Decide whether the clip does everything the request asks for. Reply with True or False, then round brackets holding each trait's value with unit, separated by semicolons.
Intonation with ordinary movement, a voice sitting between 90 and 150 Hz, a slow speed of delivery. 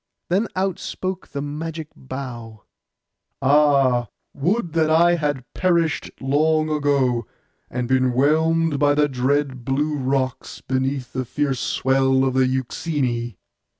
True (3.2 semitones; 140 Hz; 125 wpm)